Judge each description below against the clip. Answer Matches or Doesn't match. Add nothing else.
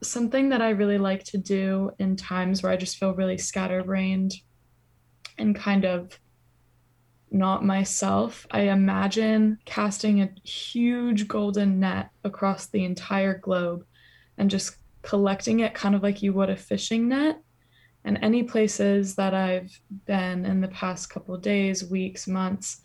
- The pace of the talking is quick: Doesn't match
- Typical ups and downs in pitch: Doesn't match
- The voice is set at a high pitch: Matches